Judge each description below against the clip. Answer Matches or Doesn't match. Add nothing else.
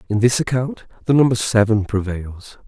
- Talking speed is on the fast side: Doesn't match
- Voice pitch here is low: Matches